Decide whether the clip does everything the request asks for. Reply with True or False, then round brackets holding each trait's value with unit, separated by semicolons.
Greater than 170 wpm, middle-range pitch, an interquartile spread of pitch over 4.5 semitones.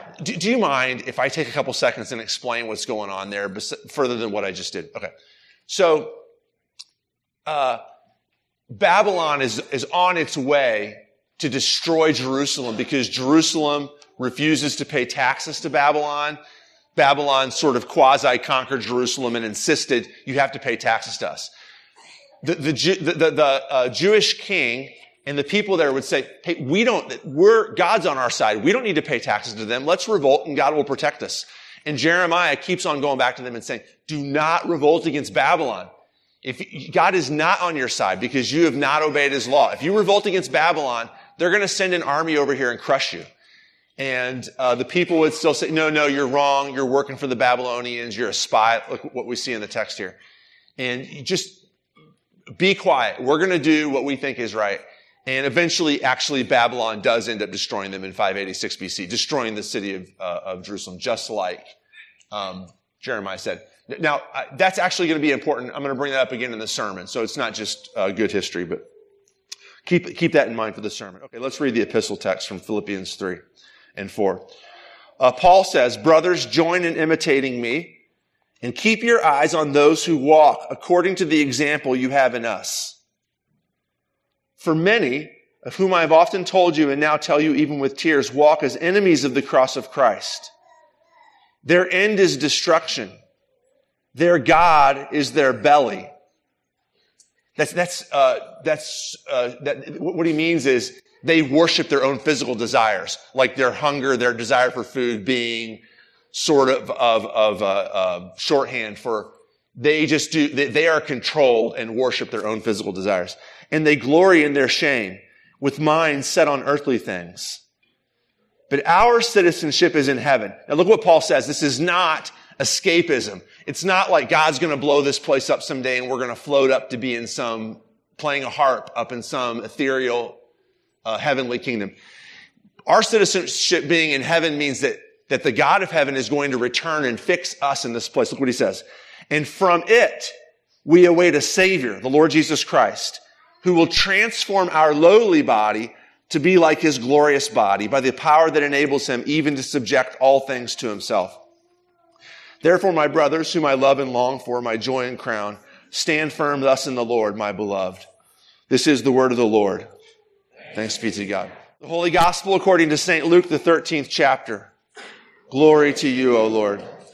True (185 wpm; 145 Hz; 5.2 semitones)